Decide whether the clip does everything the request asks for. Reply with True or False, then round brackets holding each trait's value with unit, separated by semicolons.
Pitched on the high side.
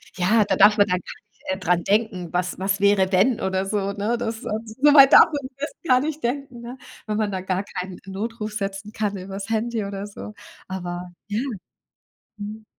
True (205 Hz)